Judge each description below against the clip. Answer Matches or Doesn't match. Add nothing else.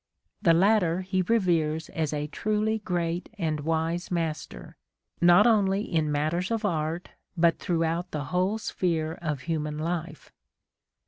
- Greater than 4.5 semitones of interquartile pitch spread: Doesn't match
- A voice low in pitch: Doesn't match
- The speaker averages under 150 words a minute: Matches